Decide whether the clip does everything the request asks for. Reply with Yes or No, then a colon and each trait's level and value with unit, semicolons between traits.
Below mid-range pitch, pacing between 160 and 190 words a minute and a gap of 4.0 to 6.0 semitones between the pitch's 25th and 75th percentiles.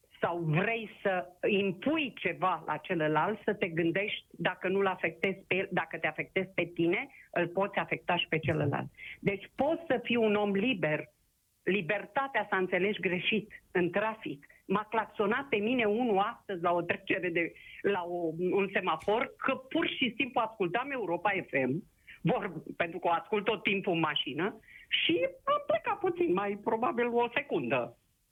No: high, 195 Hz; average, 165 wpm; average, 4.4 semitones